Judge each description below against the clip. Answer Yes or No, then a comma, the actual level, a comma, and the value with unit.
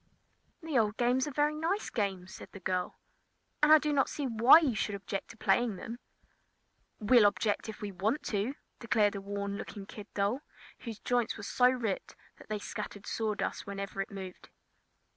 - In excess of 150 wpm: Yes, average, 180 wpm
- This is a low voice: No, high, 215 Hz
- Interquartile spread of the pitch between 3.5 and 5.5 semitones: Yes, average, 3.9 semitones